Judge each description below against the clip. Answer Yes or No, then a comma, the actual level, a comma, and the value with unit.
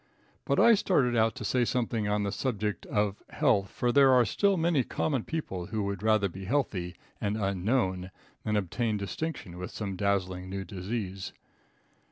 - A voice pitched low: Yes, low, 105 Hz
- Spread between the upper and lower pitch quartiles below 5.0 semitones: Yes, average, 4.2 semitones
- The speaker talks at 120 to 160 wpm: No, average, 170 wpm